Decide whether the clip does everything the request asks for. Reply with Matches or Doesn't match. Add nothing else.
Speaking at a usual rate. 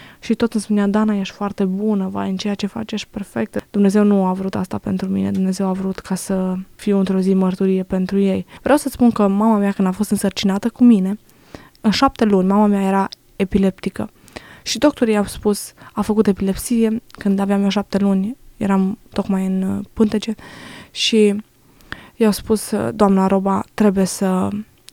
Doesn't match